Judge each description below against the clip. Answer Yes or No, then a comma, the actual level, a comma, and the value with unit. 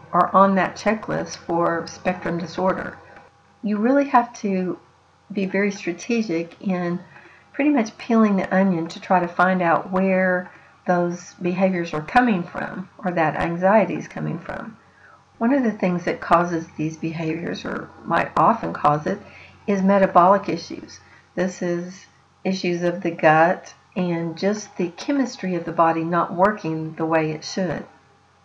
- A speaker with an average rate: Yes, average, 150 wpm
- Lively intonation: No, average, 2.8 semitones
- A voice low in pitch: No, medium, 180 Hz